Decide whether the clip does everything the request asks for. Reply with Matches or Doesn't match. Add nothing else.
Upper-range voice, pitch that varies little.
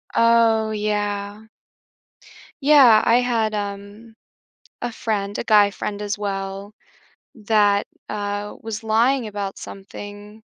Matches